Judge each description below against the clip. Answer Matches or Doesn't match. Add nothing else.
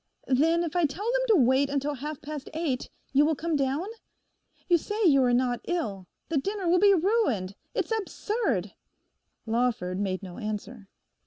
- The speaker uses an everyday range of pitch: Doesn't match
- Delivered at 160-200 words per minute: Matches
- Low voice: Doesn't match